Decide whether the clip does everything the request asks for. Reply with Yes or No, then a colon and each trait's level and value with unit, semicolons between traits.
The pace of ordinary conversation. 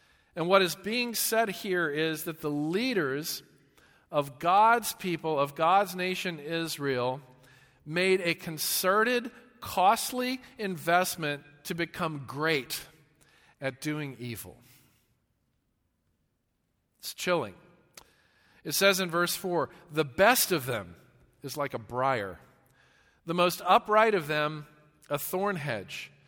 No: slow, 115 wpm